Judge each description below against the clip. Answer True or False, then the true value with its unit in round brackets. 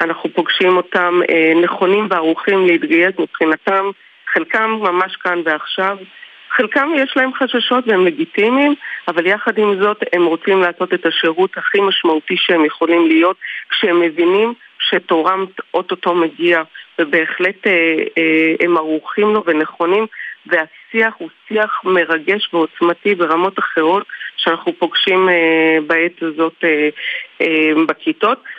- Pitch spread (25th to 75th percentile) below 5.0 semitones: True (3.4 semitones)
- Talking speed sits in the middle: True (115 wpm)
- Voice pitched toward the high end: False (175 Hz)